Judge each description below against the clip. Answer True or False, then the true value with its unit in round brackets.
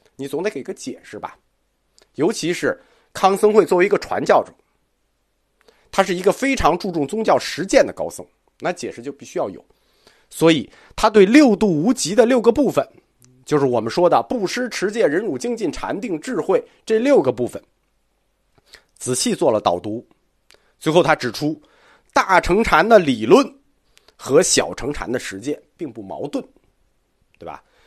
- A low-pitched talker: False (185 Hz)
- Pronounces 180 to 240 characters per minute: True (235 characters per minute)